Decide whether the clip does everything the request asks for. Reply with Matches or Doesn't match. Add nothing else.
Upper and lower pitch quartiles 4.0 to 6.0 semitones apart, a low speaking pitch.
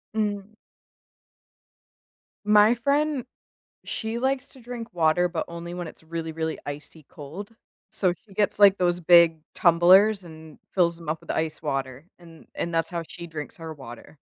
Doesn't match